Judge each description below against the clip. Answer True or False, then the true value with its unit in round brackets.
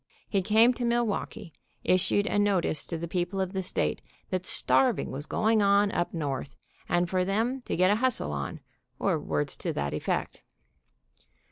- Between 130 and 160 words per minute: False (170 wpm)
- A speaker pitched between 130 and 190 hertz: True (185 Hz)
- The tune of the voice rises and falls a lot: False (4.2 semitones)